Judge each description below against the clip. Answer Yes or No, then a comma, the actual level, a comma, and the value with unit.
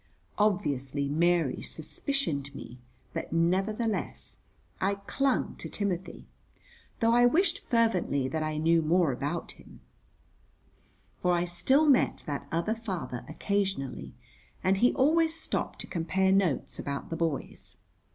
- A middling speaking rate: No, slow, 125 wpm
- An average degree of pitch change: No, wide, 6.4 semitones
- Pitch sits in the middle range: Yes, medium, 180 Hz